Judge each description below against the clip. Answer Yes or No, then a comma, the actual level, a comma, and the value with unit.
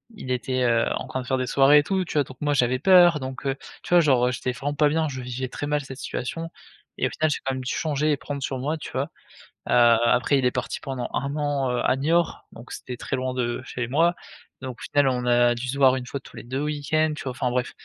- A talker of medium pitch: No, low, 130 Hz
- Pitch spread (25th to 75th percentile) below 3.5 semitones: Yes, average, 2.7 semitones